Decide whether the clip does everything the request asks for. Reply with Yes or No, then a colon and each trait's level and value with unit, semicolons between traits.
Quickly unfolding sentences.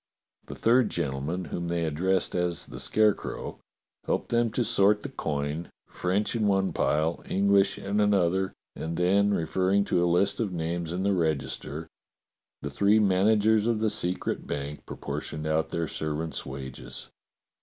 No: average, 155 wpm